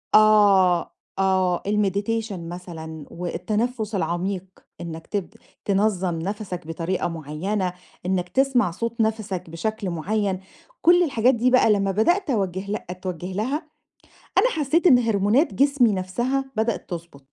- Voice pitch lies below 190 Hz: No, high, 200 Hz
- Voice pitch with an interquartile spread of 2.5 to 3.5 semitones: No, average, 4.1 semitones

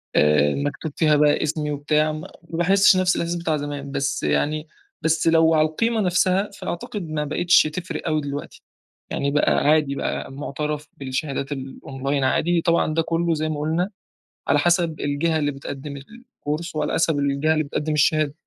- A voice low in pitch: No, medium, 155 Hz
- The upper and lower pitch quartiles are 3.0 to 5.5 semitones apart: No, narrow, 2.6 semitones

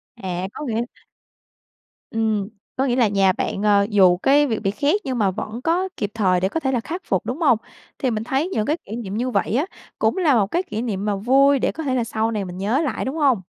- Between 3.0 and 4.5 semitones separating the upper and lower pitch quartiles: No, average, 5.2 semitones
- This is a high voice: Yes, high, 230 Hz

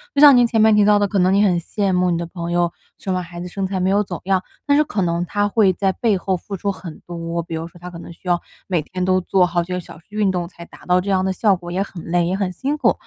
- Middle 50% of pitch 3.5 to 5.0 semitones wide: No, narrow, 2.4 semitones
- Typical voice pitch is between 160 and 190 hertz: Yes, medium, 185 Hz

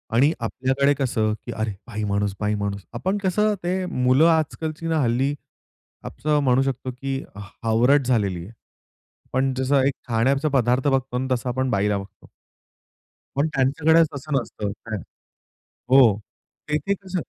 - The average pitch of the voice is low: Yes, low, 130 Hz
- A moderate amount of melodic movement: Yes, average, 4.7 semitones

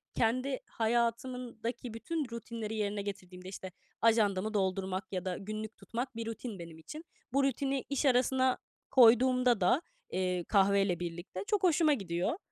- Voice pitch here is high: Yes, high, 225 Hz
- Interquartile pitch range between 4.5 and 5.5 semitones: Yes, average, 4.8 semitones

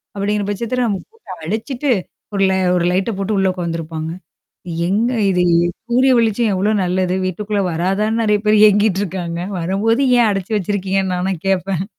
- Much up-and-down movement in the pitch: No, average, 2.8 semitones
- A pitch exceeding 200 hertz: No, high, 195 Hz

